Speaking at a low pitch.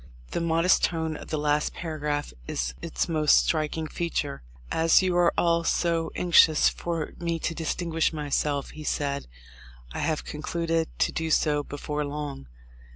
No: medium, 160 Hz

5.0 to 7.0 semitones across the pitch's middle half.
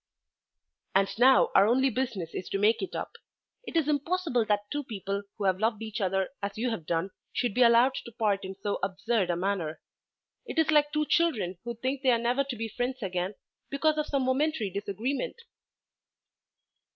Yes: wide, 5.4 semitones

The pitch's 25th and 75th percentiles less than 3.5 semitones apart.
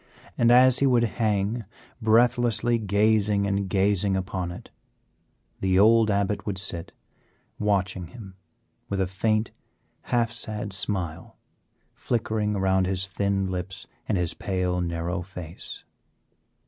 Yes: average, 2.7 semitones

